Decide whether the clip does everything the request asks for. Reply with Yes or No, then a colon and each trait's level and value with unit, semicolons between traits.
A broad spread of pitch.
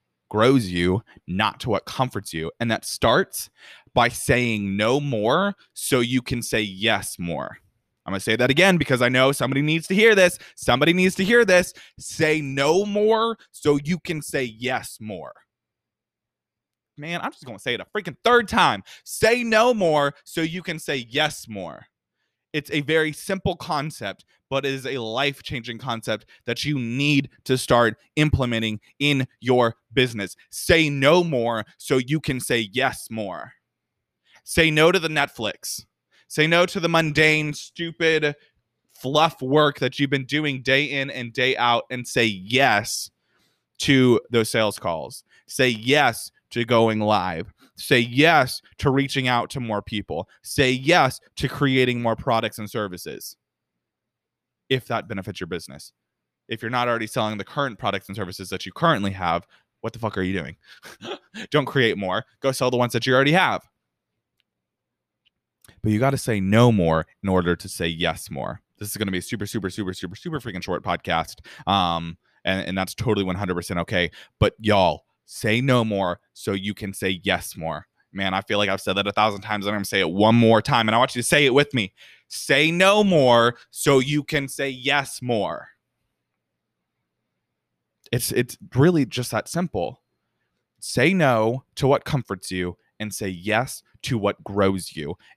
Yes: wide, 5.8 semitones